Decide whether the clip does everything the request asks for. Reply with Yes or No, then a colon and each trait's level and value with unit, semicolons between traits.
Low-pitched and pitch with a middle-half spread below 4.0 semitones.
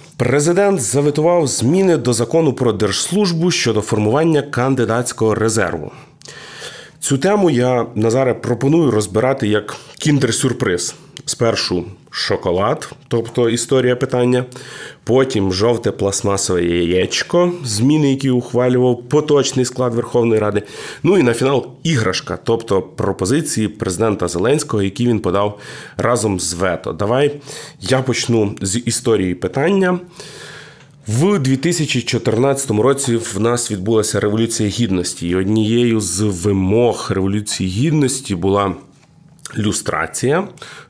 No: low, 120 Hz; average, 4.7 semitones